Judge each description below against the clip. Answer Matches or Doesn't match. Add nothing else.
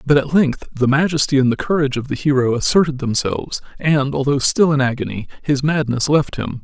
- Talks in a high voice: Doesn't match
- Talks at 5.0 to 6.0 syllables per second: Matches